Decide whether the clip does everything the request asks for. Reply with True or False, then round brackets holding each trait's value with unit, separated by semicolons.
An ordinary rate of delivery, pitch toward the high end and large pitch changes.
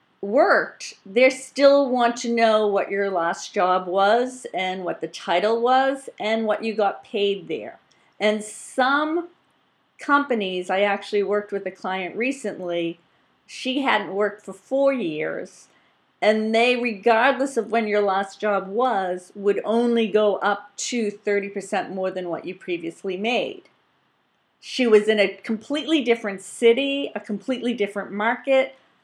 False (145 wpm; 210 Hz; 3.6 semitones)